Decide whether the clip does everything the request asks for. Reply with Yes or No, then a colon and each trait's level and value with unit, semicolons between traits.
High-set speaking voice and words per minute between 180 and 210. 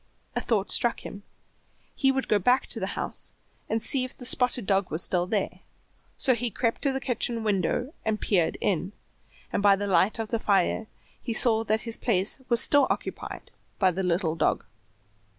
Yes: high, 220 Hz; average, 190 wpm